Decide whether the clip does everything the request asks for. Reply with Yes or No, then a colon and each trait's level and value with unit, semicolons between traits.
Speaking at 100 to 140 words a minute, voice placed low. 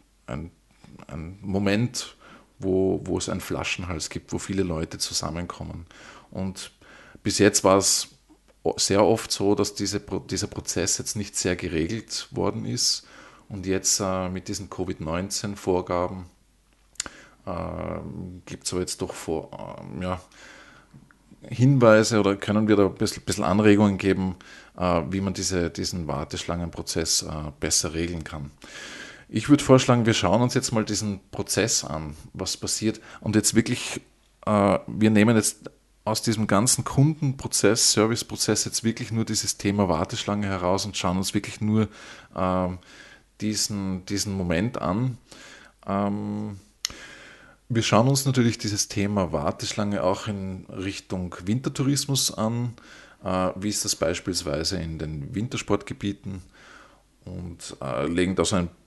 Yes: average, 130 wpm; low, 100 Hz